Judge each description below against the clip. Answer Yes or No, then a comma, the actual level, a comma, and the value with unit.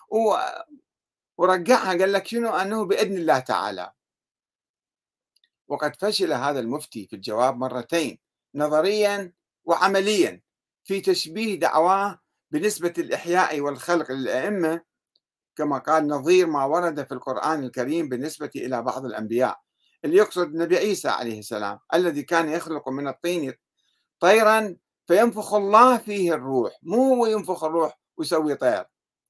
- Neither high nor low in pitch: Yes, medium, 180 Hz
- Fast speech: No, average, 115 wpm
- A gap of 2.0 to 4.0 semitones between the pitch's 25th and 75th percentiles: No, average, 5.2 semitones